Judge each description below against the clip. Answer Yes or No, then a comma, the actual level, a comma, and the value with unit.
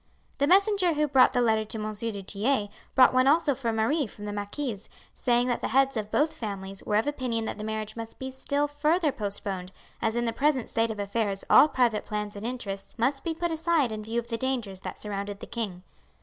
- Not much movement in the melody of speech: No, average, 4.6 semitones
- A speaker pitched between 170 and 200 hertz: No, high, 230 Hz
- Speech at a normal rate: No, fast, 225 wpm